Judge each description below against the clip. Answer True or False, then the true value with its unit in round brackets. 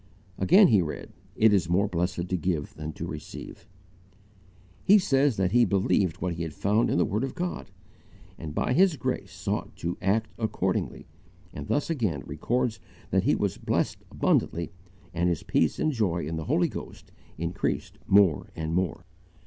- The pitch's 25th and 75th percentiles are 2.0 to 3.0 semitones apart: False (5.6 semitones)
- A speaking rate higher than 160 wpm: True (170 wpm)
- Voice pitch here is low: True (95 Hz)